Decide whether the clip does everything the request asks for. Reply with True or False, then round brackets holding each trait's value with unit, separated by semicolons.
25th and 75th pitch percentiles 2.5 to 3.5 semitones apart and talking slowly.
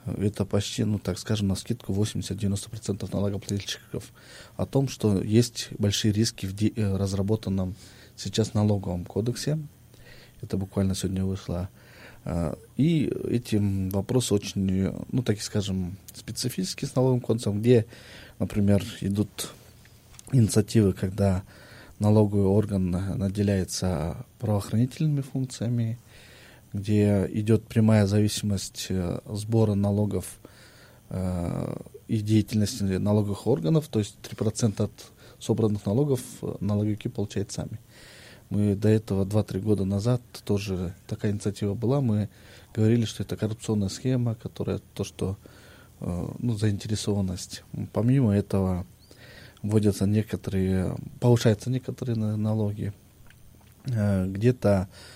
True (2.9 semitones; 100 wpm)